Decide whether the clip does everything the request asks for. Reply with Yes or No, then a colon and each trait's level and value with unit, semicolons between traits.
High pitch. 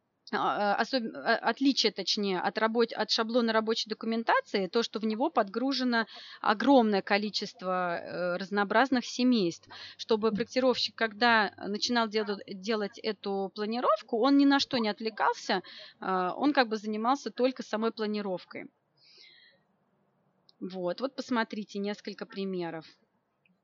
Yes: high, 220 Hz